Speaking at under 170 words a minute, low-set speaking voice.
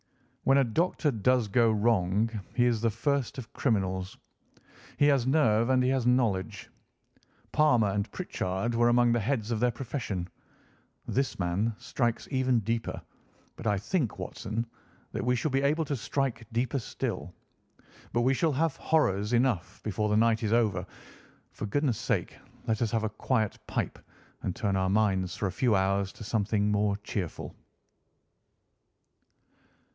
Yes: average, 160 wpm; low, 115 Hz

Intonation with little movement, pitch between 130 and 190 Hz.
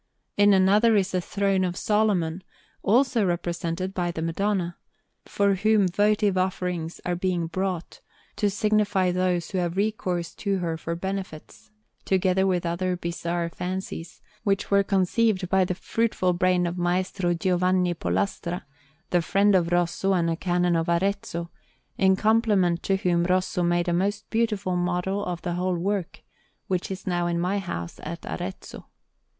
Yes: narrow, 2.2 semitones; medium, 185 Hz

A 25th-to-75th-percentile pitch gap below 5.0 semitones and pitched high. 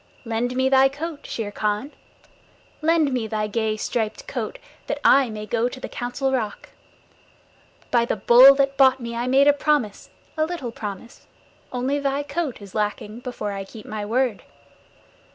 Yes: average, 4.1 semitones; high, 245 Hz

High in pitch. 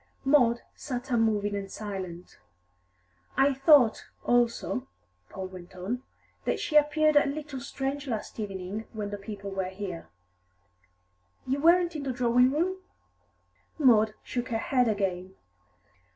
Yes: high, 235 Hz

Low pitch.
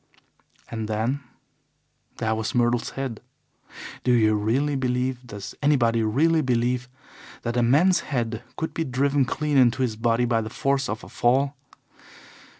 Yes: low, 125 Hz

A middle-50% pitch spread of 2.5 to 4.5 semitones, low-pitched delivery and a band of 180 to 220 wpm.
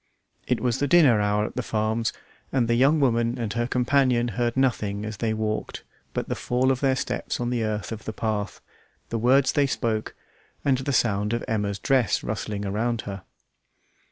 Yes: average, 2.9 semitones; low, 115 Hz; average, 190 wpm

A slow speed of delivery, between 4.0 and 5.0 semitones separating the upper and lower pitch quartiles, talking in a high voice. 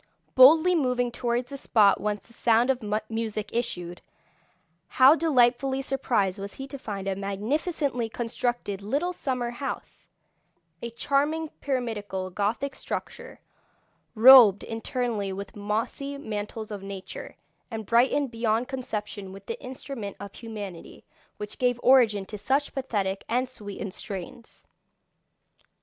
Yes: slow, 125 wpm; average, 4.3 semitones; high, 235 Hz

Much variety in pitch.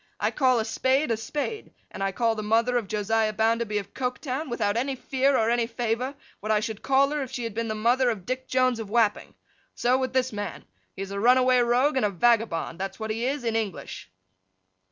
No: average, 3.0 semitones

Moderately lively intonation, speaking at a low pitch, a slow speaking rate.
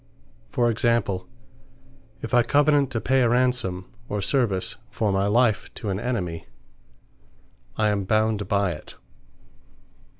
Yes: average, 3.6 semitones; low, 110 Hz; slow, 130 wpm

